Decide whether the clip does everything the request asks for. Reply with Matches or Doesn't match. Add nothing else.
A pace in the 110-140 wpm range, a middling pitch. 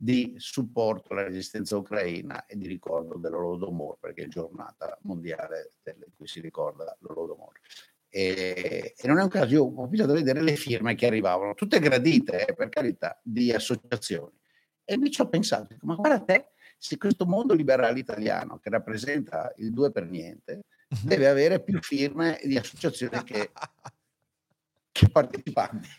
Doesn't match